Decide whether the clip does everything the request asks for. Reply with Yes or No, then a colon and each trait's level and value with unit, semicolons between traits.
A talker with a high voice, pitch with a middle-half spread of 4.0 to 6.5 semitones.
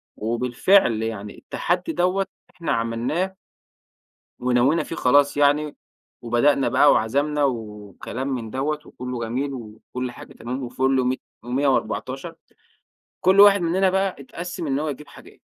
No: low, 135 Hz; average, 4.6 semitones